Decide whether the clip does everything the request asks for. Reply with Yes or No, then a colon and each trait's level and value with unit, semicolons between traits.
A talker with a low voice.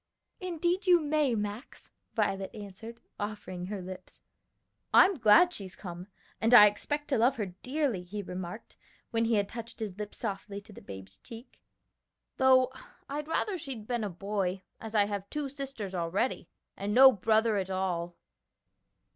No: high, 215 Hz